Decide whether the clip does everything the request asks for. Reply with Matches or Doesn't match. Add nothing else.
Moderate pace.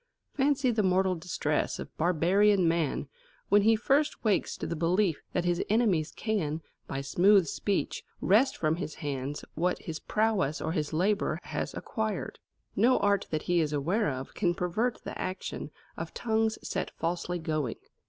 Matches